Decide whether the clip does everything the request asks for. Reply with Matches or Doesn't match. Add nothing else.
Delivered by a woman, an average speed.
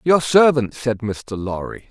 Doesn't match